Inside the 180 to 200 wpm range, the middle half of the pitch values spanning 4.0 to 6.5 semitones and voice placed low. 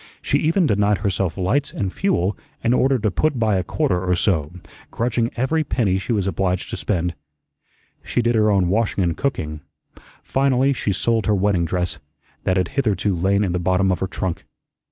Yes: average, 190 wpm; average, 4.4 semitones; low, 100 Hz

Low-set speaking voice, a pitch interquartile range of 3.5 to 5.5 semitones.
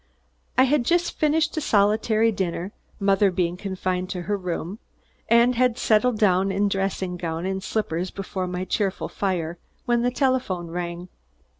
No: high, 195 Hz; average, 4.2 semitones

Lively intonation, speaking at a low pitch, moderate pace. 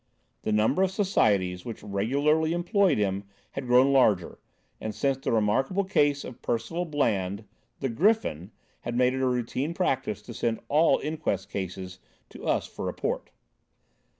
Yes: wide, 6.5 semitones; low, 125 Hz; average, 150 wpm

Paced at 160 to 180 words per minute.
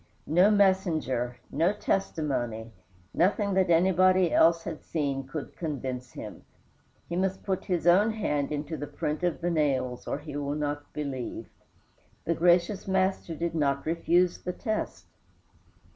No: average, 145 wpm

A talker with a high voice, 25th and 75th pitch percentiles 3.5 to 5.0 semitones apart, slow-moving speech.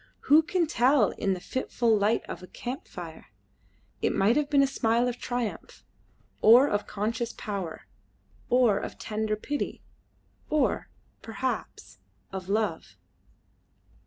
Yes: high, 230 Hz; average, 3.8 semitones; slow, 130 wpm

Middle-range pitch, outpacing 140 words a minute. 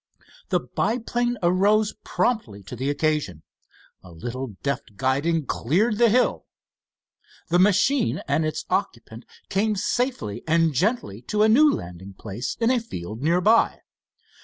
No: medium, 165 Hz; slow, 135 wpm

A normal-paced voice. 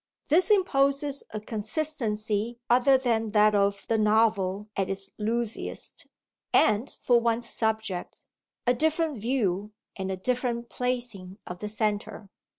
No: slow, 130 wpm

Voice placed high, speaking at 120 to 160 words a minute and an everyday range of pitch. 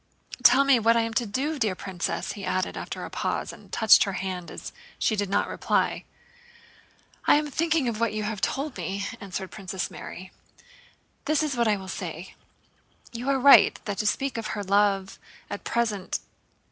No: high, 215 Hz; average, 190 wpm; average, 4.4 semitones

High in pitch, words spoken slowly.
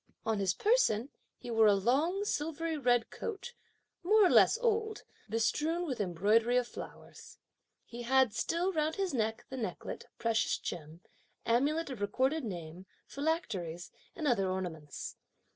No: high, 245 Hz; average, 145 wpm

